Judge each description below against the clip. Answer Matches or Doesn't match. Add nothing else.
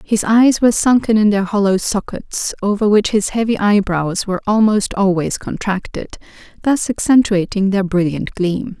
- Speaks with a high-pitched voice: Matches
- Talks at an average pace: Matches